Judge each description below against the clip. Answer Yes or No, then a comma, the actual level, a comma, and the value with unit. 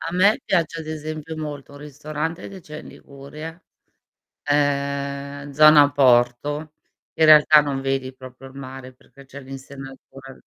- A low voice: No, medium, 145 Hz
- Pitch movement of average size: No, narrow, 2.3 semitones